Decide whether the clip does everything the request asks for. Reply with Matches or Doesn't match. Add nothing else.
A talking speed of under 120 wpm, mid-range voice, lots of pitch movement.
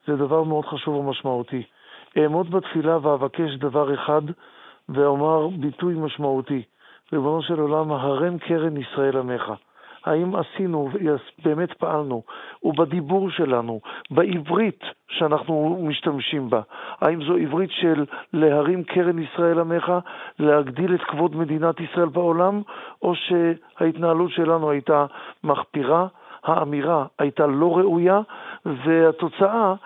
Doesn't match